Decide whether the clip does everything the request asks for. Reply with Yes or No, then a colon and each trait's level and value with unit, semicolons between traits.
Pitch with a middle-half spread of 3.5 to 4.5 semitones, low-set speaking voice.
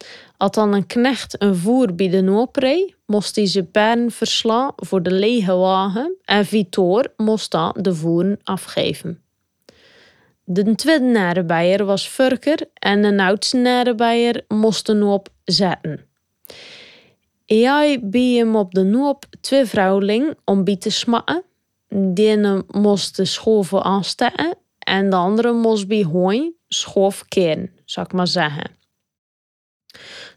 No: average, 4.0 semitones; high, 205 Hz